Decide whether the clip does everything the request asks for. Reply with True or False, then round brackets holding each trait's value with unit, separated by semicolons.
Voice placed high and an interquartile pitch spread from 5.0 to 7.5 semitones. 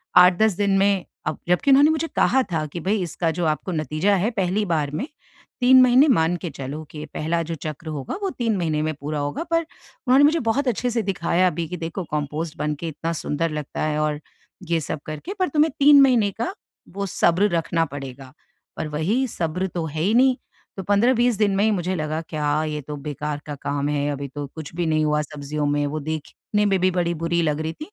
False (165 Hz; 5.3 semitones)